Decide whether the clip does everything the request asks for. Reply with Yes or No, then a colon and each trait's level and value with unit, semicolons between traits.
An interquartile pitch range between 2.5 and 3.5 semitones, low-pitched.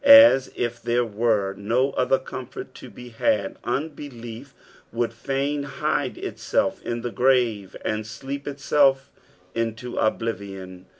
Yes: average, 3.2 semitones; low, 120 Hz